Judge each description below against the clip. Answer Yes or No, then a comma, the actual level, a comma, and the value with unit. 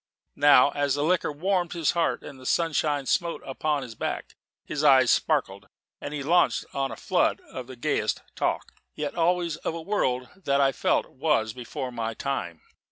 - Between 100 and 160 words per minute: No, average, 185 wpm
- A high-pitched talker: No, medium, 145 Hz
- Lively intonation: No, average, 4.0 semitones